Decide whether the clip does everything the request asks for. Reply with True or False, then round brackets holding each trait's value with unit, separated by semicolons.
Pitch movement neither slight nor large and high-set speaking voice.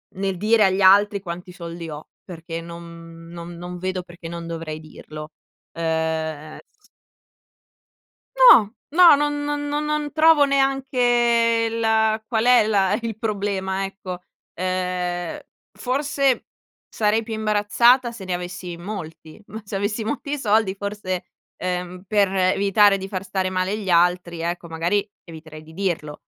True (4.5 semitones; 195 Hz)